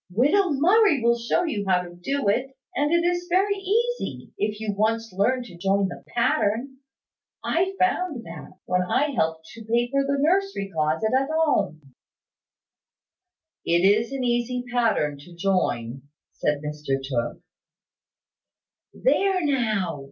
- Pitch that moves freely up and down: Yes, wide, 8.7 semitones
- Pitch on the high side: Yes, high, 235 Hz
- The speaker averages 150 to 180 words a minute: No, average, 140 wpm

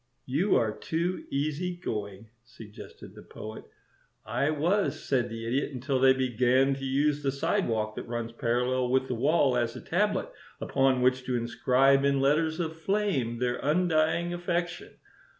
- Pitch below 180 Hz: Yes, low, 135 Hz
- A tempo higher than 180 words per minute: No, average, 155 wpm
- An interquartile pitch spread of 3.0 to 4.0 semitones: No, average, 4.4 semitones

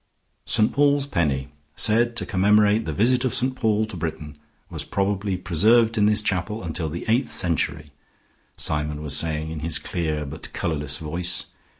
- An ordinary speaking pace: Yes, average, 165 wpm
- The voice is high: No, very low, 90 Hz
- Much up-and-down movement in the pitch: Yes, wide, 5.8 semitones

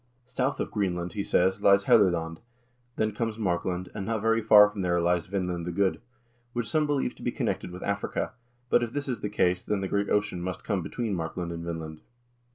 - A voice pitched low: Yes, low, 100 Hz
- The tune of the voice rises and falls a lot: No, average, 3.3 semitones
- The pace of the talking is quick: Yes, fast, 210 wpm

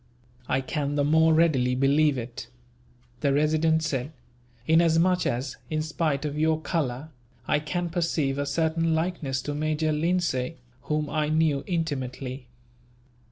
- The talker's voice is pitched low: No, medium, 155 Hz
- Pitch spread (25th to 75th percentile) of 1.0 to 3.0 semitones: Yes, average, 2.7 semitones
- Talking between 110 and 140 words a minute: Yes, slow, 135 wpm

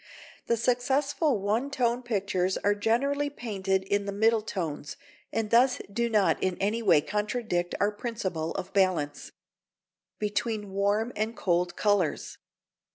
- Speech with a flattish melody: No, average, 3.6 semitones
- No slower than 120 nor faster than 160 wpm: Yes, average, 140 wpm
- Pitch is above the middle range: Yes, high, 210 Hz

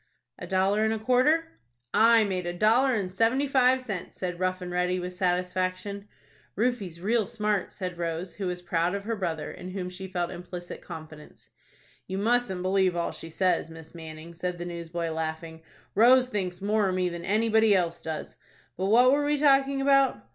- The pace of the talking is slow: No, average, 185 wpm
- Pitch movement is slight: No, average, 4.2 semitones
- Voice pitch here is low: No, medium, 185 Hz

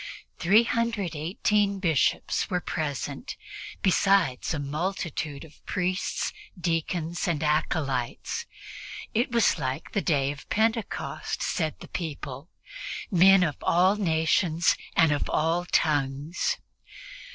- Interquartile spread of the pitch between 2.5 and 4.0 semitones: No, average, 4.4 semitones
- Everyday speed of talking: No, slow, 110 wpm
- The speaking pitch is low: No, medium, 165 Hz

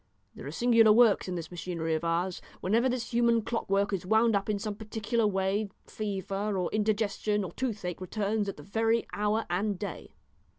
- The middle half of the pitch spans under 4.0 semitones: Yes, average, 2.8 semitones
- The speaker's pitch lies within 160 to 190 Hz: No, high, 205 Hz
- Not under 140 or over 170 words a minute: No, average, 180 wpm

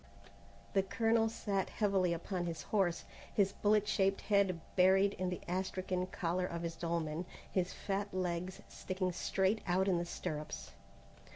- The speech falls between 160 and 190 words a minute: No, average, 150 wpm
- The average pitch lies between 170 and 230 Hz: Yes, medium, 185 Hz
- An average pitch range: No, narrow, 2.2 semitones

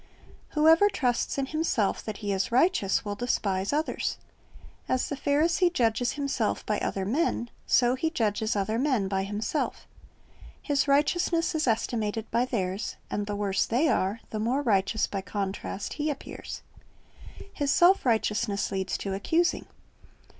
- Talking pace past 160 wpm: No, average, 145 wpm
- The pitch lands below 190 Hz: No, high, 235 Hz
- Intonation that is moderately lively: No, wide, 6.1 semitones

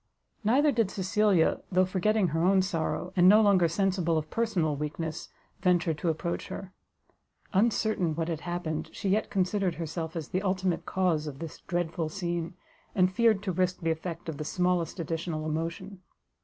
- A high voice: No, medium, 180 Hz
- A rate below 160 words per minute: No, average, 170 wpm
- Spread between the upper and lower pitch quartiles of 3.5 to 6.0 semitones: No, average, 2.9 semitones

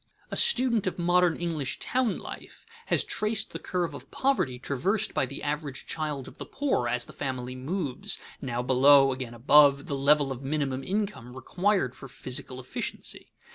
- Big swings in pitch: Yes, wide, 5.7 semitones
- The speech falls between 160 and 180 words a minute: Yes, average, 170 wpm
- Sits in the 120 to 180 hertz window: Yes, medium, 140 Hz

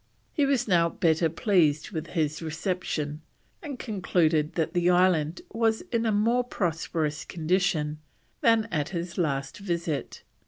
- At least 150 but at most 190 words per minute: No, slow, 135 wpm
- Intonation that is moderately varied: Yes, average, 4.5 semitones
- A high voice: No, medium, 170 Hz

